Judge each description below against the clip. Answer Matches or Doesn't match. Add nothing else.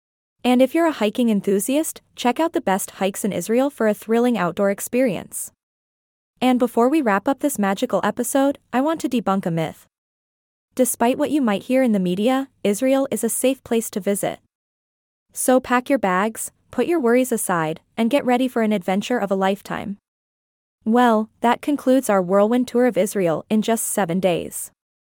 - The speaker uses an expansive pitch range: Doesn't match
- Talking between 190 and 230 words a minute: Doesn't match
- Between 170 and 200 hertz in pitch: Doesn't match